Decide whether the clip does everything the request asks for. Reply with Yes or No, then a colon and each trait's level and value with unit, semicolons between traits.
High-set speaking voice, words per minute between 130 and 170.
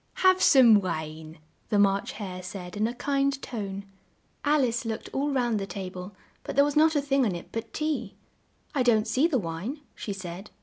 No: high, 225 Hz; fast, 205 wpm